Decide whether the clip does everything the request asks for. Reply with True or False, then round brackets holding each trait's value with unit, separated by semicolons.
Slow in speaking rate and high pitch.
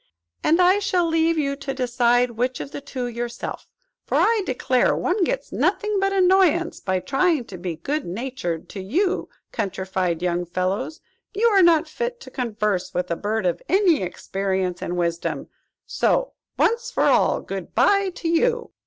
False (170 wpm; 260 Hz)